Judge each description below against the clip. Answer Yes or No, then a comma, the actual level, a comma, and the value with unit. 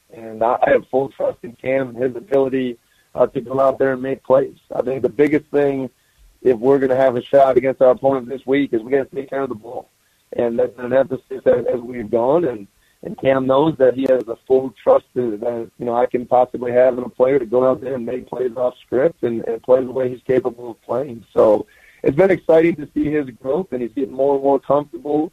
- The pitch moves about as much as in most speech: No, narrow, 1.7 semitones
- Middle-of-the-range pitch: No, low, 130 Hz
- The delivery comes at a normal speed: No, fast, 245 wpm